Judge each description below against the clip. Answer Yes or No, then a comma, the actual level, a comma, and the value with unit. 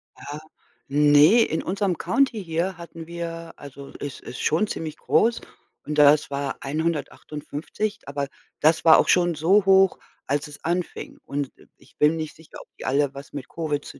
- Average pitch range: Yes, average, 3.2 semitones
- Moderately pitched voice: Yes, medium, 160 Hz